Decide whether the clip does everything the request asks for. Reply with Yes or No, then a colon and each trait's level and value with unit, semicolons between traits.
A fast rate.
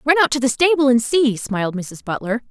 Yes: fast, 240 wpm